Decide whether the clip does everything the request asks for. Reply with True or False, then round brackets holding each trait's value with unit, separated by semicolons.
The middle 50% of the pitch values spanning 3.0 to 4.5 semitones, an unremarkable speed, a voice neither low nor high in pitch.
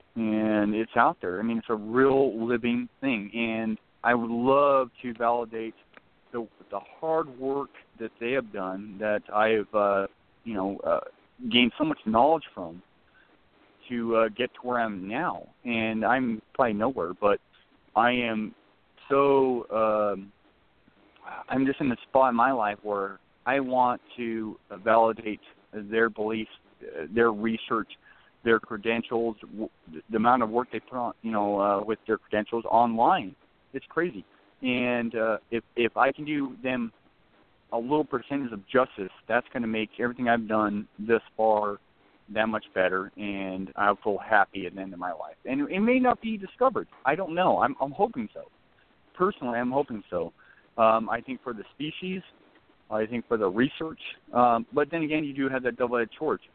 False (3.5 semitones; 170 wpm; 115 Hz)